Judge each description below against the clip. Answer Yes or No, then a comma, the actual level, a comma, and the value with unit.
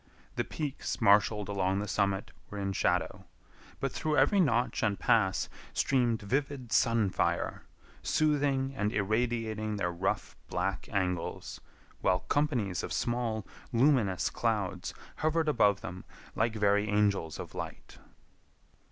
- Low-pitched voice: Yes, low, 105 Hz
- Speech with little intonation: No, average, 4.3 semitones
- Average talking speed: No, slow, 125 wpm